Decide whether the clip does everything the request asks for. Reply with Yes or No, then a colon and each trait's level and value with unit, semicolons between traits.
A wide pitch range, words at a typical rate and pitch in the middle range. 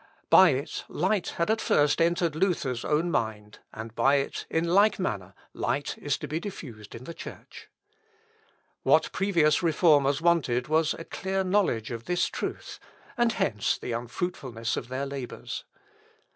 Yes: wide, 6.3 semitones; average, 155 wpm; medium, 150 Hz